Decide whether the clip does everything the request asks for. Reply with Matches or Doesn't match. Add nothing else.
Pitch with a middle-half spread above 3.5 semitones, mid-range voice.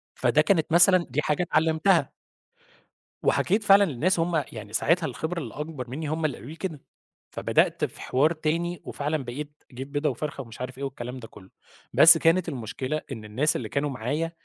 Matches